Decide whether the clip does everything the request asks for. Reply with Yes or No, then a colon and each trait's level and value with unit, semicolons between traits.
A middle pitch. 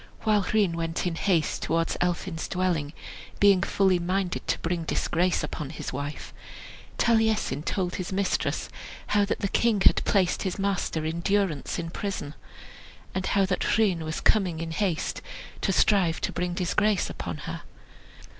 Yes: medium, 180 Hz